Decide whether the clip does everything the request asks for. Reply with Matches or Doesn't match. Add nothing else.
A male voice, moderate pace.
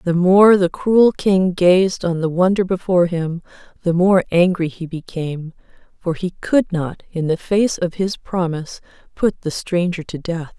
Doesn't match